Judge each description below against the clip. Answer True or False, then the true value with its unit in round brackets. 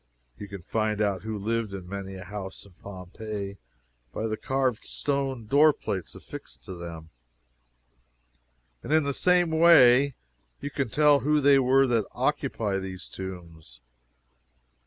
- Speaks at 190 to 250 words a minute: False (145 wpm)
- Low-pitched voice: True (110 Hz)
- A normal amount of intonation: False (6.3 semitones)